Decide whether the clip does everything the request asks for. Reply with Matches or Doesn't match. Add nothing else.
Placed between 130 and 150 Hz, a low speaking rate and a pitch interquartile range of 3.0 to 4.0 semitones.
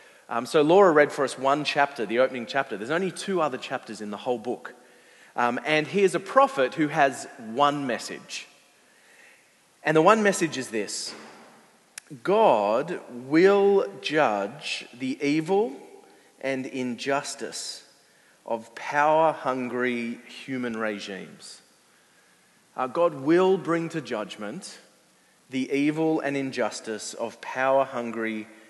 Doesn't match